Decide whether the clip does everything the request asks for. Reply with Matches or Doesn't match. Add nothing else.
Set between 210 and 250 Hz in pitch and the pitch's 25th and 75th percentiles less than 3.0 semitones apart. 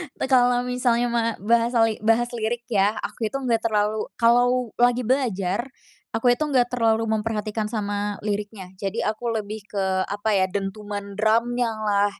Matches